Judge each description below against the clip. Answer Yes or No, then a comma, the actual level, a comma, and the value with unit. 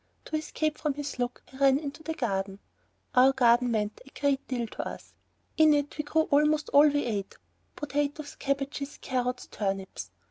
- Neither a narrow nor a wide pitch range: Yes, average, 3.3 semitones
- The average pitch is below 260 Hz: No, very high, 275 Hz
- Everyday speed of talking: Yes, average, 180 wpm